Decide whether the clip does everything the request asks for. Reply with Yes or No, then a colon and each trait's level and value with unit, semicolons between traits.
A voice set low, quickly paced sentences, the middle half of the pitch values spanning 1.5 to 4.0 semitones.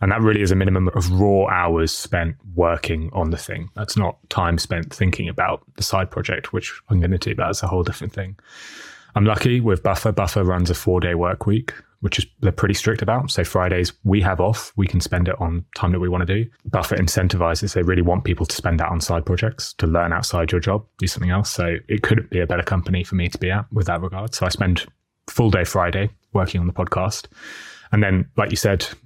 Yes: very low, 95 Hz; fast, 235 wpm; average, 3.2 semitones